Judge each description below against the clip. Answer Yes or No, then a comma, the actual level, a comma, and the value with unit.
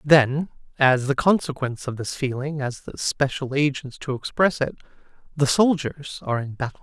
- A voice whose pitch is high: No, medium, 140 Hz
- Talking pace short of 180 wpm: Yes, average, 165 wpm